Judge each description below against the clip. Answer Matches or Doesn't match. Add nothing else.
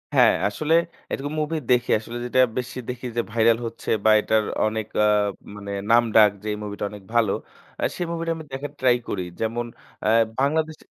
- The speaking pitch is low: Matches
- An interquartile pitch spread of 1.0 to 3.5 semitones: Doesn't match